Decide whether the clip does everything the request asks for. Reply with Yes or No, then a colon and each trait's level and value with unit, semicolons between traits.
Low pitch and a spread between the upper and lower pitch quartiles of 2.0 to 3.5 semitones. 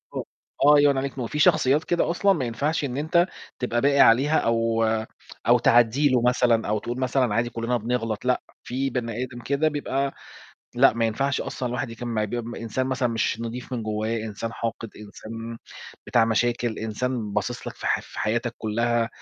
Yes: low, 120 Hz; average, 2.7 semitones